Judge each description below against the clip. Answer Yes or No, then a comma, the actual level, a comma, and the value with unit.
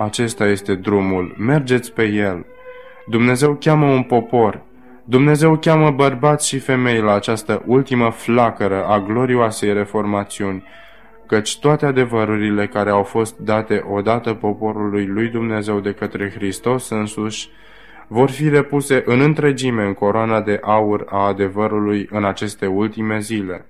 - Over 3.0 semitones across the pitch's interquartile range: Yes, average, 3.8 semitones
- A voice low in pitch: Yes, low, 110 Hz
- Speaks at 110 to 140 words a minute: Yes, average, 130 wpm